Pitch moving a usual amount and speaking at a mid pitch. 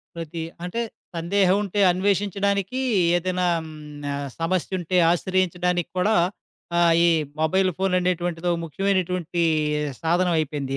No: narrow, 2.2 semitones; medium, 180 Hz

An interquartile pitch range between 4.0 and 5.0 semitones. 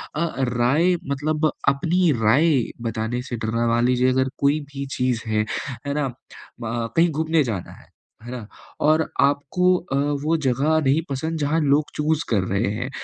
Yes: average, 4.5 semitones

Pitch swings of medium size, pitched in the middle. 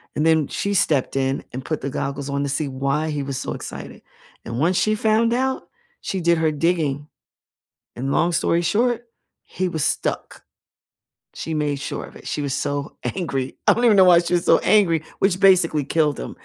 Yes: average, 4.7 semitones; medium, 160 Hz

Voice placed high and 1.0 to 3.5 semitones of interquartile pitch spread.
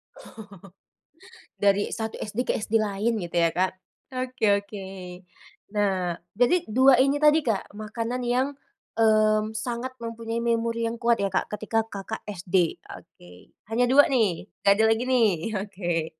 Yes: high, 220 Hz; average, 3.0 semitones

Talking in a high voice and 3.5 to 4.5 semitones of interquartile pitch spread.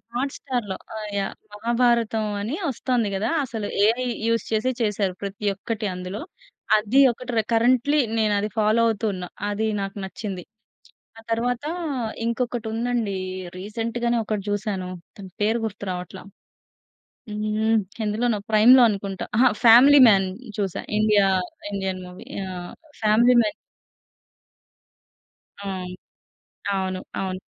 No: high, 215 Hz; average, 3.1 semitones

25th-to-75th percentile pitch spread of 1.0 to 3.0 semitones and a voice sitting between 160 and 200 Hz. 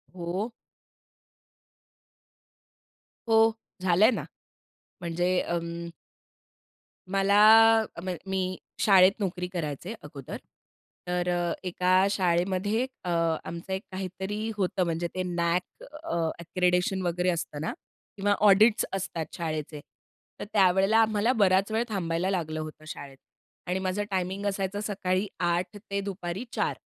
Yes: narrow, 2.5 semitones; medium, 185 Hz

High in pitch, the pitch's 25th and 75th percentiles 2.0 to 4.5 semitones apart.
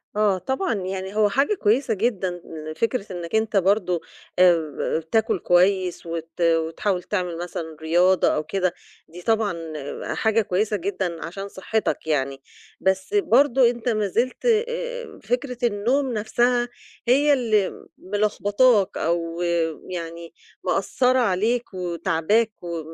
No: high, 200 Hz; average, 5.1 semitones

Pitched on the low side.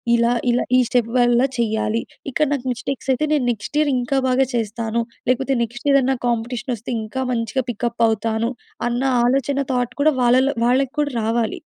No: high, 245 Hz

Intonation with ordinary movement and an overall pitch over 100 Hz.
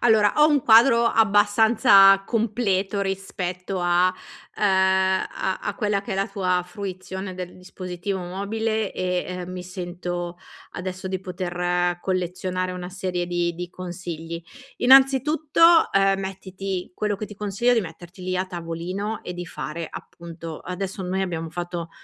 No: narrow, 2.3 semitones; medium, 185 Hz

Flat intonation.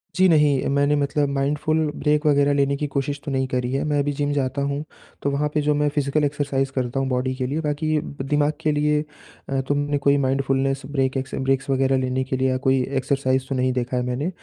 Yes: narrow, 1.8 semitones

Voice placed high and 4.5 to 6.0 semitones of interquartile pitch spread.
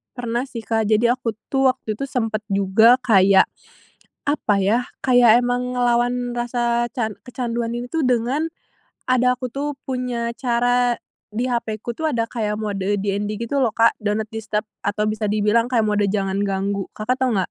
No: high, 235 Hz; average, 2.7 semitones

